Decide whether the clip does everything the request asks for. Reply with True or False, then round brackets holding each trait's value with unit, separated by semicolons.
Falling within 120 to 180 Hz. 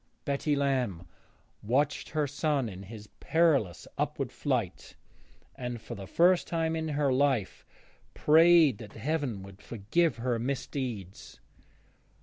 True (135 Hz)